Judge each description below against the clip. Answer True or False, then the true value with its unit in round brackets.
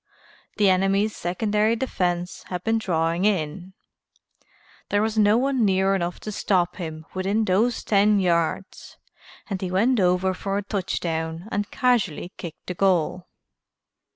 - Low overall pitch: False (190 Hz)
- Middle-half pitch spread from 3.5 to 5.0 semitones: False (3.0 semitones)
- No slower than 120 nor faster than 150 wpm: True (140 wpm)